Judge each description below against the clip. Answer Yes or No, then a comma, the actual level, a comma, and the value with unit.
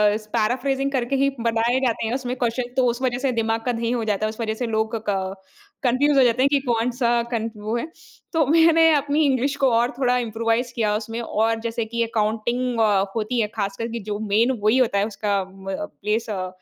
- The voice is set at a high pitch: Yes, high, 230 Hz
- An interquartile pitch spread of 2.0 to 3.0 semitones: Yes, narrow, 2.5 semitones